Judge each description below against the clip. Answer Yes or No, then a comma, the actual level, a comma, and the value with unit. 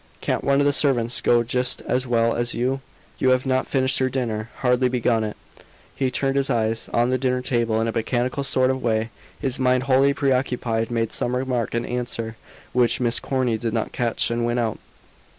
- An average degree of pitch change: No, narrow, 1.9 semitones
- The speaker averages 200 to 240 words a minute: Yes, fast, 205 wpm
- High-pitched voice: No, low, 125 Hz